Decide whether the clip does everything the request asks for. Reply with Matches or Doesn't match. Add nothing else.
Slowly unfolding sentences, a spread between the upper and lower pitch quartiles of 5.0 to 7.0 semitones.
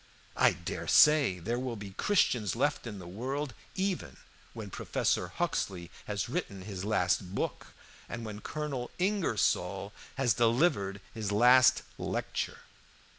Matches